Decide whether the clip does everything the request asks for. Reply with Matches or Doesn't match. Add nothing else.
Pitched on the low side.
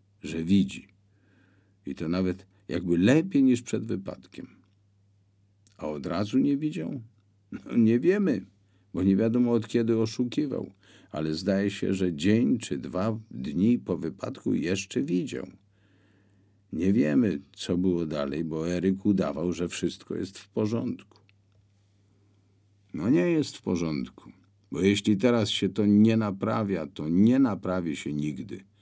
Matches